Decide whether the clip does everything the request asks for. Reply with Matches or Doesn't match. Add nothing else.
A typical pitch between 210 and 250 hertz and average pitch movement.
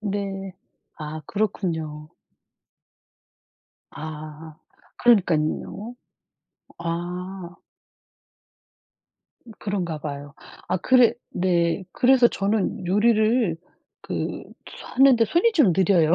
Doesn't match